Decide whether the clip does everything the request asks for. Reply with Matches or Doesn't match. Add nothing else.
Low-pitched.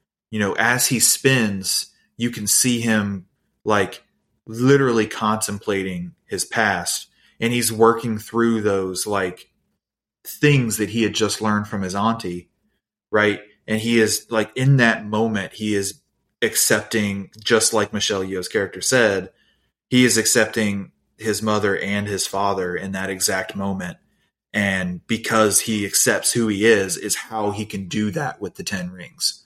Matches